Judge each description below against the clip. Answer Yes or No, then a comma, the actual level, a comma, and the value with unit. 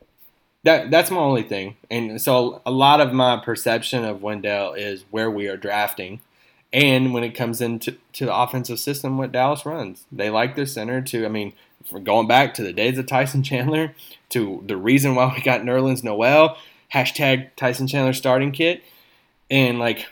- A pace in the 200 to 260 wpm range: No, average, 180 wpm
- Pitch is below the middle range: Yes, low, 125 Hz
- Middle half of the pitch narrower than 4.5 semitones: Yes, average, 3.1 semitones